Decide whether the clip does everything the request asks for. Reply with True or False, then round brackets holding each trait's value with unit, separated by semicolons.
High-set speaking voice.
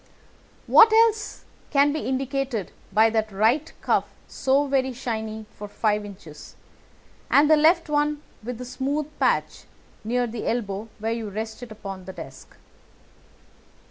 True (240 Hz)